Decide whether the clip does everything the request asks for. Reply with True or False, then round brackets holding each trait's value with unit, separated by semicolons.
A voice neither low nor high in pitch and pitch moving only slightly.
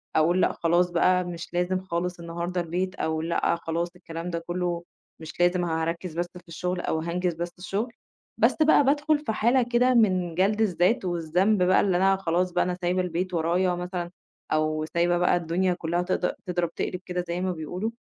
True (180 Hz; 1.5 semitones)